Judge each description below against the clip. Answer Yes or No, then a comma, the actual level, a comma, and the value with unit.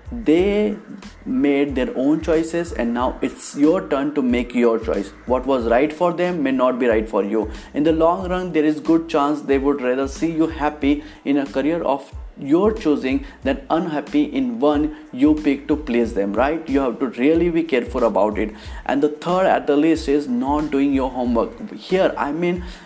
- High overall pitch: No, medium, 150 Hz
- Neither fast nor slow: No, fast, 200 wpm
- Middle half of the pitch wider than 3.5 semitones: Yes, average, 4.0 semitones